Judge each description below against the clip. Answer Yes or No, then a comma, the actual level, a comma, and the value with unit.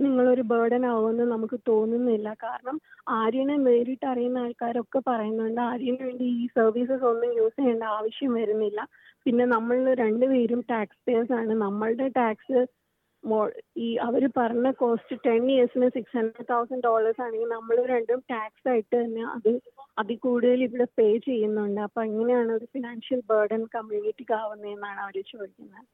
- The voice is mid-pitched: No, high, 235 Hz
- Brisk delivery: Yes, fast, 140 wpm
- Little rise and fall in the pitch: Yes, narrow, 2.0 semitones